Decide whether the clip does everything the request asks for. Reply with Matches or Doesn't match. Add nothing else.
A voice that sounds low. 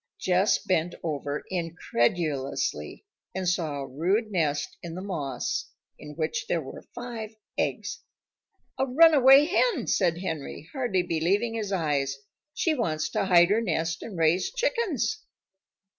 Doesn't match